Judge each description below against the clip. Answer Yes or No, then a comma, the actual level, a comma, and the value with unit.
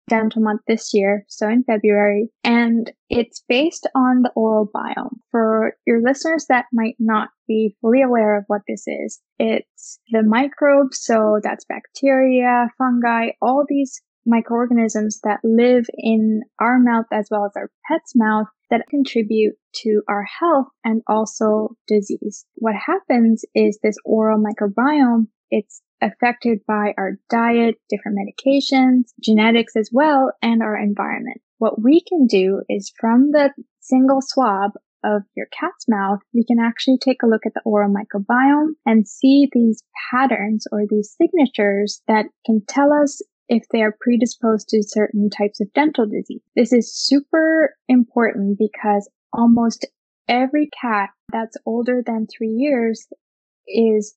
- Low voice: No, high, 230 Hz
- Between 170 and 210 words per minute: No, average, 150 wpm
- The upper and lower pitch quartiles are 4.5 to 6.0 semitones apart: No, average, 3.2 semitones